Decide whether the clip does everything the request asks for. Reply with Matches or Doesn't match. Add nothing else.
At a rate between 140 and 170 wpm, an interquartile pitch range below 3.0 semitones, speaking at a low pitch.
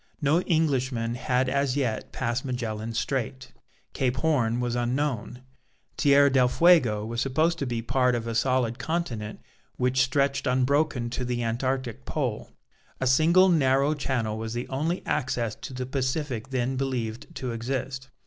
Matches